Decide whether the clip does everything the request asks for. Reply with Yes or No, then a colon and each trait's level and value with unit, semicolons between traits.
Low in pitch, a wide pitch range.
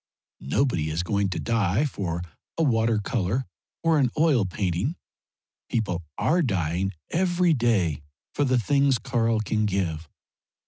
Yes: low, 110 Hz; wide, 6.7 semitones